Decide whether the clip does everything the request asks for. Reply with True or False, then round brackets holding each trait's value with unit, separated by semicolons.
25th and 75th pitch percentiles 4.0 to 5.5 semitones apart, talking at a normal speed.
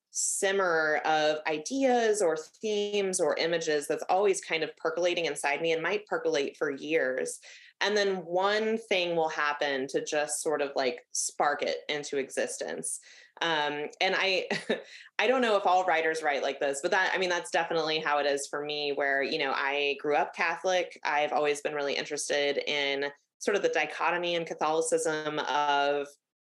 True (4.5 semitones; 175 wpm)